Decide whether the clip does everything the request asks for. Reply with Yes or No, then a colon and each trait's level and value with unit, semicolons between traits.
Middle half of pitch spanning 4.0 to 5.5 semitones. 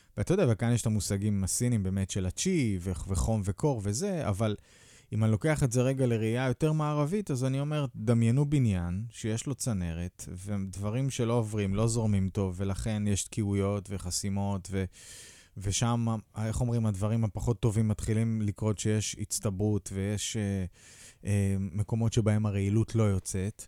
No: average, 3.1 semitones